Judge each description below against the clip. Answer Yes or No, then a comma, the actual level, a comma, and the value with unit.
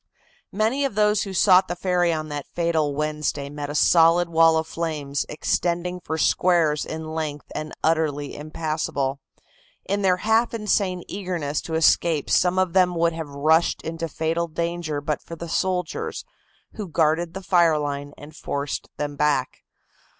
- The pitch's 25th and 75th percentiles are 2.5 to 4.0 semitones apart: Yes, average, 2.9 semitones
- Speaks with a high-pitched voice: No, medium, 165 Hz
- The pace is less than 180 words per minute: Yes, average, 160 wpm